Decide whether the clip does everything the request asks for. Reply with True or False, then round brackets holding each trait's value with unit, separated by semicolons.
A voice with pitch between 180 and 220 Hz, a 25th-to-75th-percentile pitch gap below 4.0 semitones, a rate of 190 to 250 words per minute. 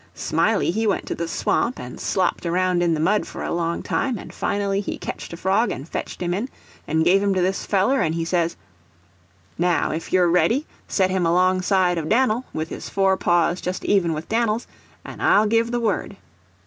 True (185 Hz; 3.4 semitones; 200 wpm)